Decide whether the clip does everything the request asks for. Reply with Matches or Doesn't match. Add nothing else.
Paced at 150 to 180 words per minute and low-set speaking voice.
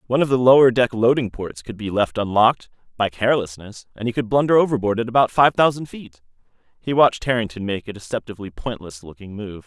Doesn't match